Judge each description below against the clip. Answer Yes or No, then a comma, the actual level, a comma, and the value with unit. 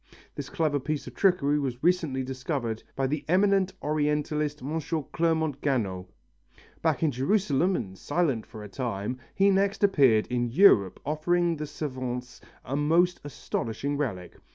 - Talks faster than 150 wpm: No, average, 145 wpm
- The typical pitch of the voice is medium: Yes, medium, 145 Hz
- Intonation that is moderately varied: Yes, average, 4.6 semitones